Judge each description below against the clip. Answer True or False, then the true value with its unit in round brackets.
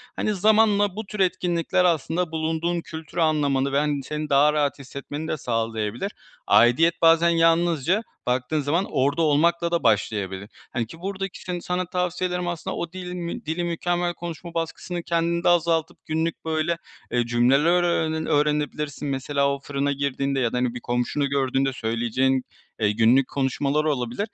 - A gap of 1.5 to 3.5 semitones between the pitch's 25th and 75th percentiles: False (4.2 semitones)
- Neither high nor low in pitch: True (155 Hz)